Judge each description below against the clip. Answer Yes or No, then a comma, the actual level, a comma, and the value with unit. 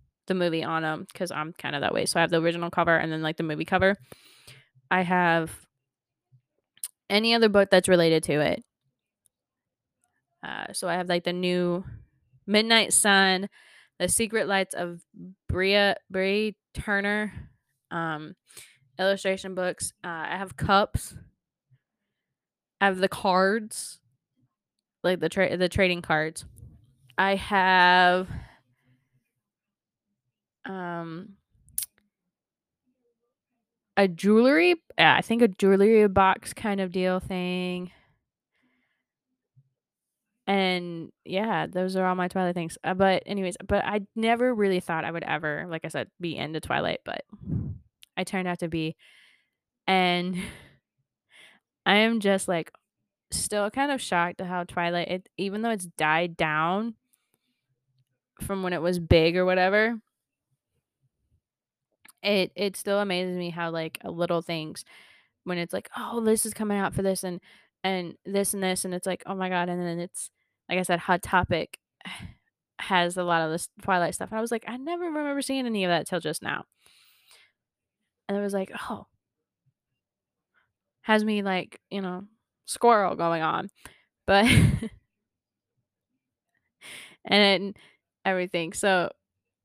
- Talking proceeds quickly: No, average, 140 wpm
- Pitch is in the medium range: Yes, medium, 180 Hz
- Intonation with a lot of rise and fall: No, average, 3.3 semitones